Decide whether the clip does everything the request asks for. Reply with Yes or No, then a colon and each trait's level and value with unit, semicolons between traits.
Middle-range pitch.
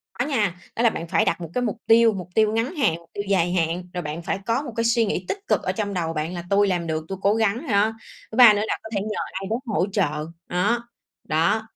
No: high, 200 Hz